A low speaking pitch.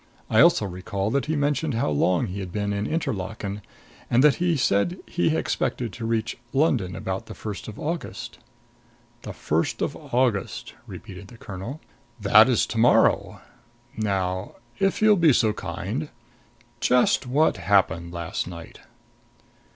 Yes: low, 110 Hz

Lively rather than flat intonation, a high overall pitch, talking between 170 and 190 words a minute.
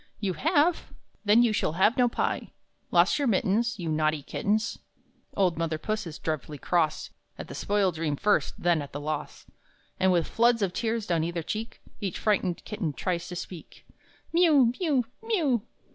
Yes: wide, 5.9 semitones; high, 195 Hz; average, 175 wpm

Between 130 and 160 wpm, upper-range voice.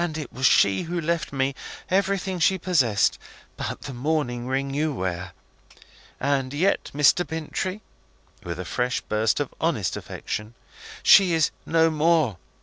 No: average, 145 wpm; medium, 145 Hz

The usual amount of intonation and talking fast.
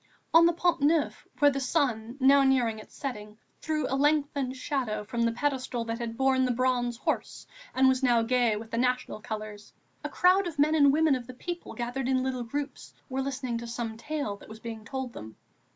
Yes: average, 3.4 semitones; fast, 210 wpm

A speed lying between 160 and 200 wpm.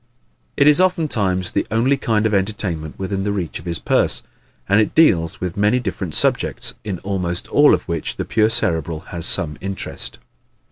Yes: average, 180 wpm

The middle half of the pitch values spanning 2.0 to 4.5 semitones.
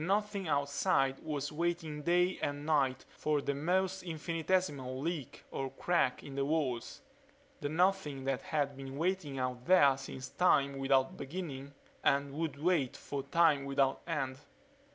Yes: average, 3.9 semitones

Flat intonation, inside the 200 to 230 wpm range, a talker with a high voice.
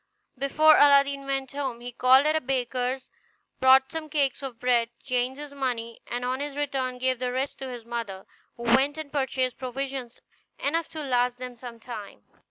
No: narrow, 2.1 semitones; average, 180 wpm; very high, 260 Hz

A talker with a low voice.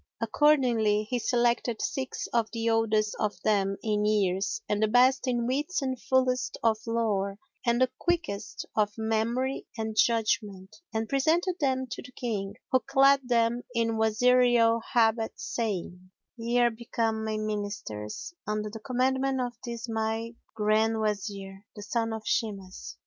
No: high, 225 Hz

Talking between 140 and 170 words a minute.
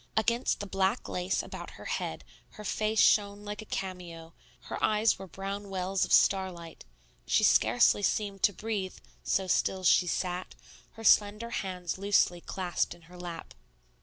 Yes: average, 160 wpm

